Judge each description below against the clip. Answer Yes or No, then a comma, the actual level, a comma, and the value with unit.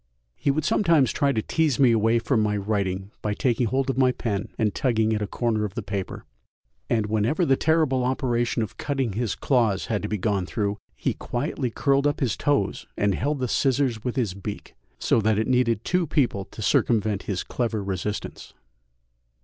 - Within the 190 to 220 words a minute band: Yes, average, 195 wpm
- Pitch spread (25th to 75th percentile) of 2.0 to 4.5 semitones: Yes, average, 4.2 semitones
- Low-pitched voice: Yes, low, 115 Hz